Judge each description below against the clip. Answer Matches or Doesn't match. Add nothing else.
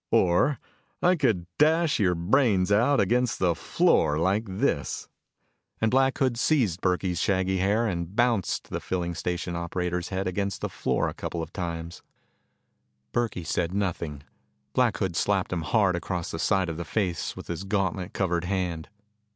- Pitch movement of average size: Matches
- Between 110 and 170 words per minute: Matches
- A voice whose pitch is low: Matches